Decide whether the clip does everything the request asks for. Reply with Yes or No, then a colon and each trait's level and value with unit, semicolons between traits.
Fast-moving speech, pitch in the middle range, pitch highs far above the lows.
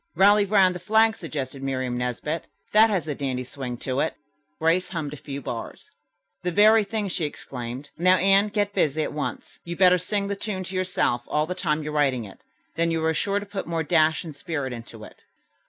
Yes: fast, 210 wpm; medium, 165 Hz; wide, 5.7 semitones